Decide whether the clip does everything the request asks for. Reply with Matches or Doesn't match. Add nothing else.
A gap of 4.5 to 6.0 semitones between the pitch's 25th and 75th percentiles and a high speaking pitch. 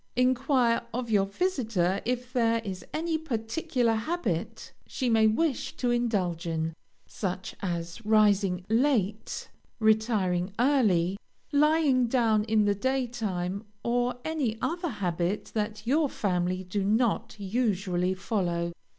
Matches